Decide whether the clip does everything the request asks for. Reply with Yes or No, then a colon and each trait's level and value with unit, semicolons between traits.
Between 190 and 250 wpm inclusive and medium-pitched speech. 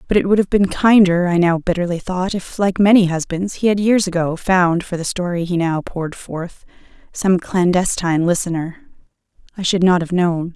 Yes: average, 195 wpm; medium, 180 Hz